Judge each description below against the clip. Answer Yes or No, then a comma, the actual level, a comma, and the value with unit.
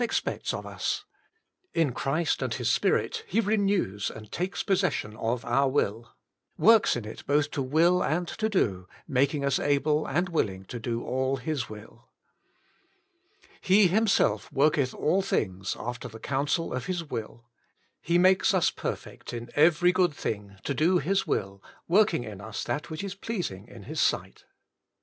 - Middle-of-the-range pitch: Yes, medium, 145 Hz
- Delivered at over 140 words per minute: Yes, average, 170 wpm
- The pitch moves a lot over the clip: Yes, wide, 7.5 semitones